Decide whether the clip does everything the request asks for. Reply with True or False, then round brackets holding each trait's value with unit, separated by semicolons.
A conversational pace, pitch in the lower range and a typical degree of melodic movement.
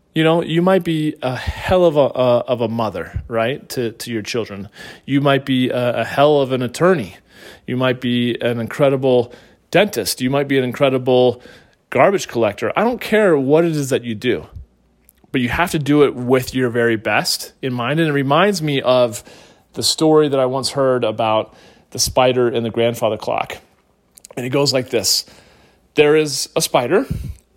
True (190 wpm; 130 Hz; 3.6 semitones)